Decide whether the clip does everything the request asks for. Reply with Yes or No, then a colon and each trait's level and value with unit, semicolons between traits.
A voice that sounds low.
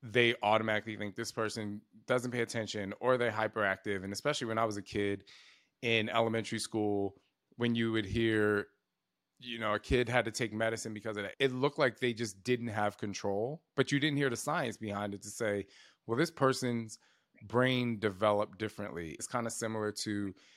Yes: low, 110 Hz